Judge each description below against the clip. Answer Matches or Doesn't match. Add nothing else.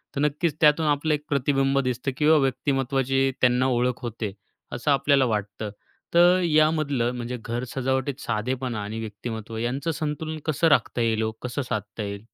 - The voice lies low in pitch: Matches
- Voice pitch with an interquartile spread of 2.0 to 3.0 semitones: Doesn't match